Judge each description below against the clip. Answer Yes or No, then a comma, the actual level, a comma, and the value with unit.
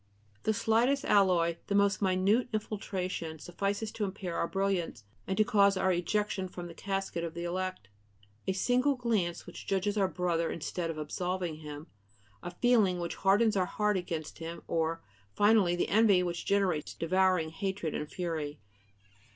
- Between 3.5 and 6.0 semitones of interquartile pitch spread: No, average, 3.1 semitones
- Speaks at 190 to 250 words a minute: No, average, 160 wpm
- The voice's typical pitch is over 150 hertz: Yes, medium, 185 Hz